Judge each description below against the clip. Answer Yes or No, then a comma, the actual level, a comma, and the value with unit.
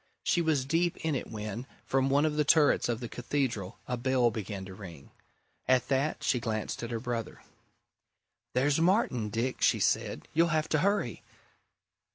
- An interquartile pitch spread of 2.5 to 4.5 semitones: No, average, 4.9 semitones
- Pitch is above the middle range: No, low, 130 Hz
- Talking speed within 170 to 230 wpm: Yes, average, 175 wpm